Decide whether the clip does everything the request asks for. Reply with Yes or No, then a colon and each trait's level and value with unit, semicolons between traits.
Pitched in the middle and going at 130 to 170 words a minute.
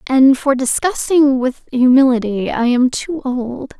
No: very high, 260 Hz; average, 140 wpm